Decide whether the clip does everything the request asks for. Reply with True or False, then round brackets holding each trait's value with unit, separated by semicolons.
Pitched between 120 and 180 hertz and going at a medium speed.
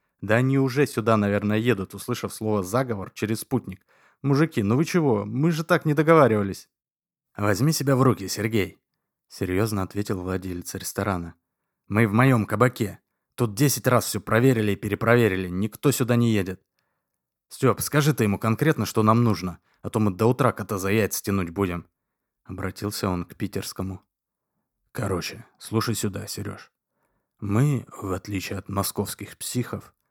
False (110 Hz; 150 wpm)